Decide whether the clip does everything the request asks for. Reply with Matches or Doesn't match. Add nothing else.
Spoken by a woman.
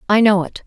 Matches